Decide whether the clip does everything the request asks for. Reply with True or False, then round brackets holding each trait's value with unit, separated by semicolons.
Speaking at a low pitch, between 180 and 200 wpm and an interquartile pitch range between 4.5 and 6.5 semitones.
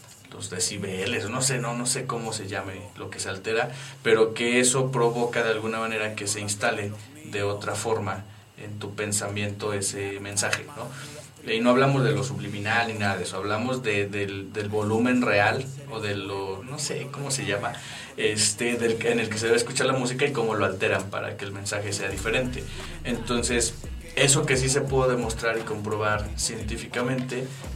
False (110 Hz; 185 wpm; 3.8 semitones)